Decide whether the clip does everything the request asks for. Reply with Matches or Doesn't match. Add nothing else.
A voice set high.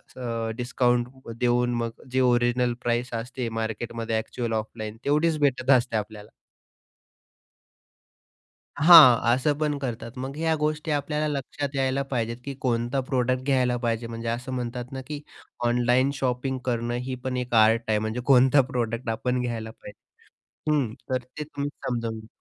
Doesn't match